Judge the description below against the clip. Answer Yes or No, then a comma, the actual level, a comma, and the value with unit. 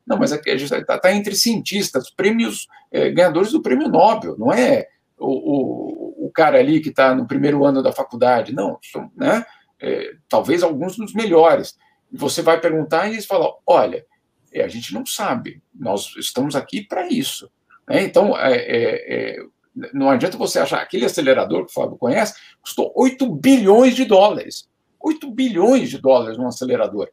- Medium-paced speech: Yes, average, 175 wpm